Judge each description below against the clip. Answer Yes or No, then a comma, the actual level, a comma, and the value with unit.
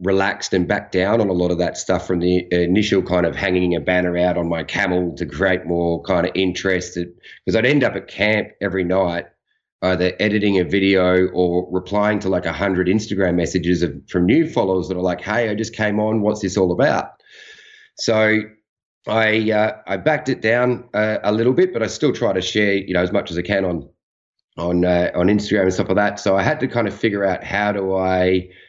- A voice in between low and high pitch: No, very low, 95 Hz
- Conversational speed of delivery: No, fast, 225 wpm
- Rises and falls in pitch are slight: No, average, 3.0 semitones